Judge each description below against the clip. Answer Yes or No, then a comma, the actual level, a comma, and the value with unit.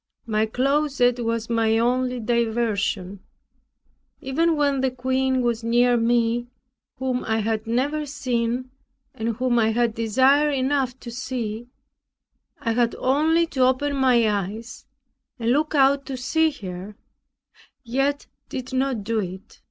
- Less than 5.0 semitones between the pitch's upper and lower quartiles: Yes, average, 2.7 semitones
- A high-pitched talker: Yes, high, 245 Hz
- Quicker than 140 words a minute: No, slow, 135 wpm